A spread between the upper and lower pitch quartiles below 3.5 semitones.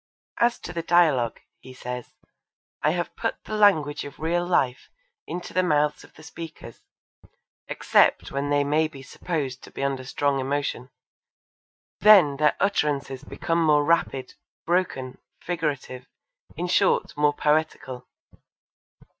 No: average, 3.9 semitones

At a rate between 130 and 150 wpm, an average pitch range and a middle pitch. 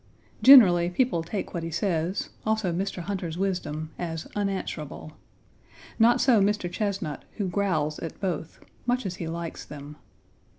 Yes: average, 140 wpm; average, 3.7 semitones; medium, 180 Hz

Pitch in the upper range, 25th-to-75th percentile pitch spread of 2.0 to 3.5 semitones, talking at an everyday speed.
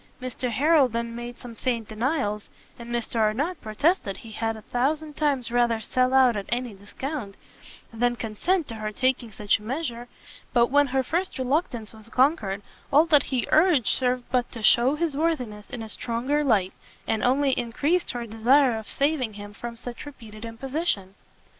No: high, 245 Hz; average, 4.0 semitones; average, 175 wpm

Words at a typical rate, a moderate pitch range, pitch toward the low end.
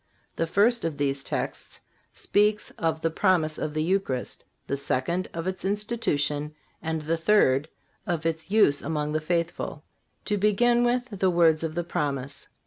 No: average, 160 wpm; average, 4.6 semitones; medium, 165 Hz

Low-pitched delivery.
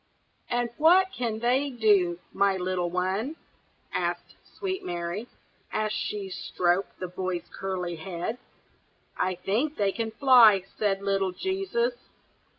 No: high, 200 Hz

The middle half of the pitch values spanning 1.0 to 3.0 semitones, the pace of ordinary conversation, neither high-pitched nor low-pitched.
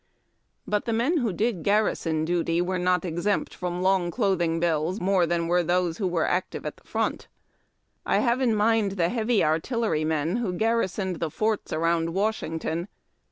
No: average, 4.3 semitones; average, 165 wpm; medium, 180 Hz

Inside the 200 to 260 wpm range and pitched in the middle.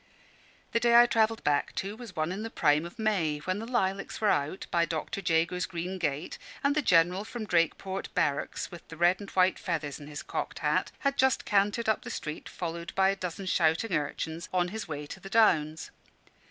Yes: fast, 205 wpm; medium, 180 Hz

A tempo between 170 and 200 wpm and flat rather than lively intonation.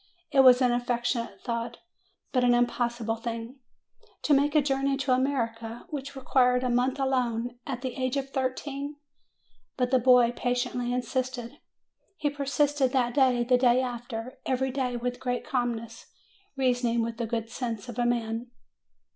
No: average, 160 wpm; narrow, 1.8 semitones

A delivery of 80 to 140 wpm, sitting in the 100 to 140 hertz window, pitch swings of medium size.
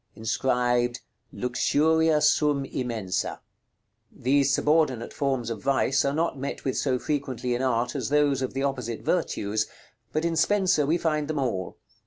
No: average, 150 wpm; low, 135 Hz; average, 3.5 semitones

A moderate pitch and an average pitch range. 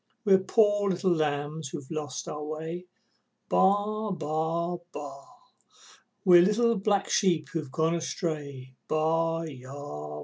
Yes: medium, 165 Hz; average, 4.1 semitones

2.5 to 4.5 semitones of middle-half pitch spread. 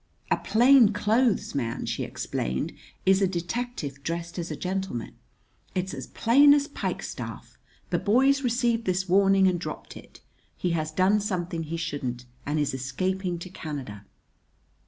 No: wide, 5.6 semitones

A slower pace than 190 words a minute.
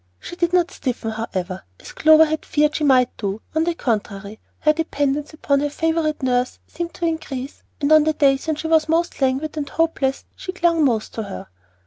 No: average, 200 wpm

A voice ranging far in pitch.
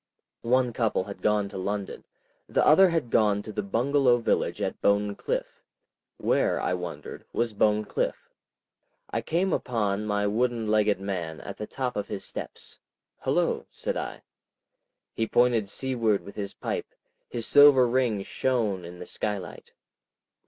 No: average, 3.5 semitones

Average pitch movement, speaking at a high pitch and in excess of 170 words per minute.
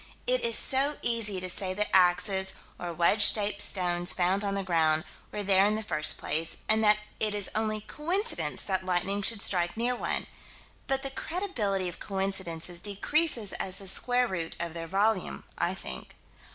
Yes: average, 3.5 semitones; high, 195 Hz; average, 180 wpm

